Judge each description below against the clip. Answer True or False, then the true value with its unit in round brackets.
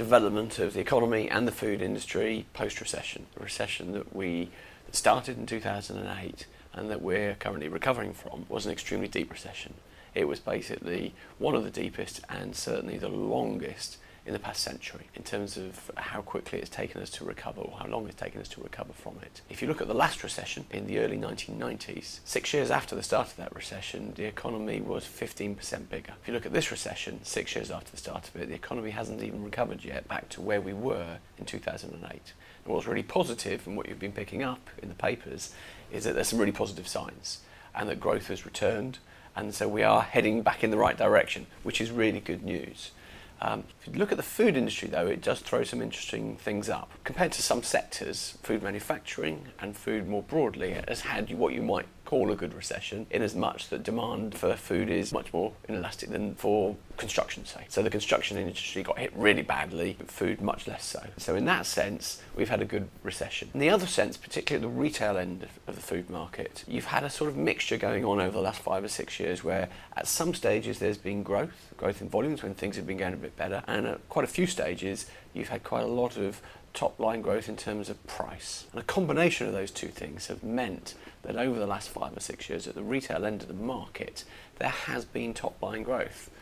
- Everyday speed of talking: False (220 wpm)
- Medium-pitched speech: False (105 Hz)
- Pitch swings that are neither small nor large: True (3.2 semitones)